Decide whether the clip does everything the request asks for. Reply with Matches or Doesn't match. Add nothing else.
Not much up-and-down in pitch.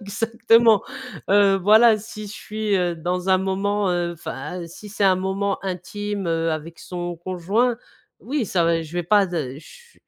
Doesn't match